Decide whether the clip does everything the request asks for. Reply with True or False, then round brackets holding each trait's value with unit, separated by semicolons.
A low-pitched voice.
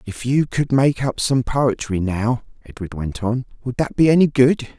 True (125 Hz)